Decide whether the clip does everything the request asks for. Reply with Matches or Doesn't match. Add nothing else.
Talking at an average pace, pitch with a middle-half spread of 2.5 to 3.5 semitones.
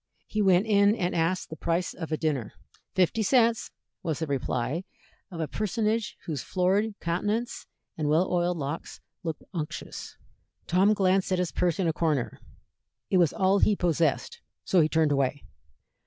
Doesn't match